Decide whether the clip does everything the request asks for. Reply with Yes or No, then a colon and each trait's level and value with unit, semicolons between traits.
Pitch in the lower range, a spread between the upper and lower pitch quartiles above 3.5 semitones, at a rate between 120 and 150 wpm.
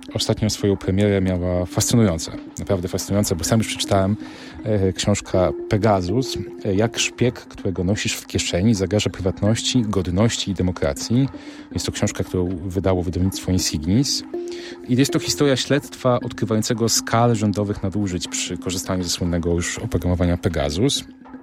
Yes: low, 105 Hz; average, 4.5 semitones; average, 135 wpm